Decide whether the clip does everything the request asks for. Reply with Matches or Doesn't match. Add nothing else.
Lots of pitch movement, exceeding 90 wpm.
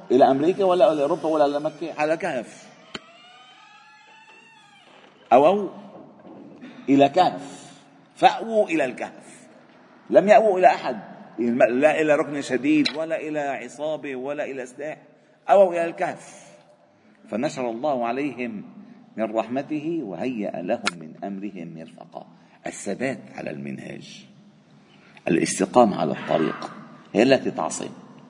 Matches